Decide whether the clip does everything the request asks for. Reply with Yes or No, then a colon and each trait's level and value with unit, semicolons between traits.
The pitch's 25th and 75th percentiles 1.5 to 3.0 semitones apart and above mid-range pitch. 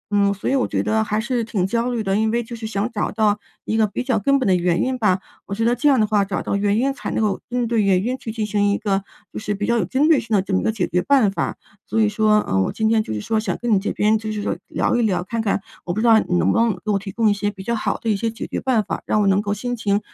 Yes: narrow, 2.4 semitones; high, 215 Hz